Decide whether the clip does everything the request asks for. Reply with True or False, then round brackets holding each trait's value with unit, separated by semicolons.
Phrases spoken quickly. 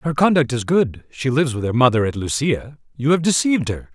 True (230 wpm)